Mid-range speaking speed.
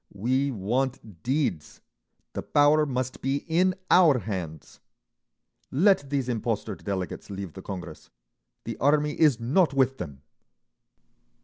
No: slow, 115 wpm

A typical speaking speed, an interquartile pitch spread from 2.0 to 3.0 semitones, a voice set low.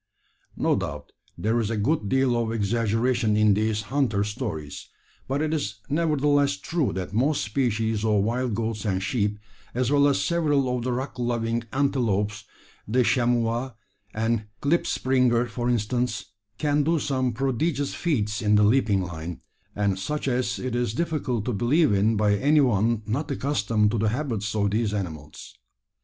No: average, 160 wpm; average, 4.1 semitones; low, 115 Hz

